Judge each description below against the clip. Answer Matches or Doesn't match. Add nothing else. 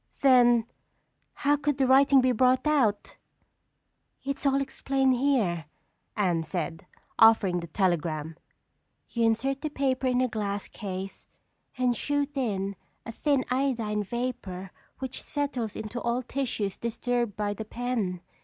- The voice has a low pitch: Doesn't match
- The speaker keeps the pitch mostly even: Doesn't match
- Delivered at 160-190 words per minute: Doesn't match